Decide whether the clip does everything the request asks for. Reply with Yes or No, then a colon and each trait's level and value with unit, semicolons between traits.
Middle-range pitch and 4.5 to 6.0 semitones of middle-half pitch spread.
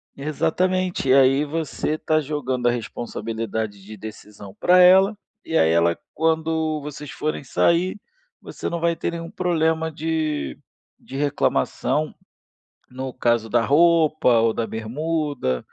Yes: medium, 150 Hz; wide, 5.5 semitones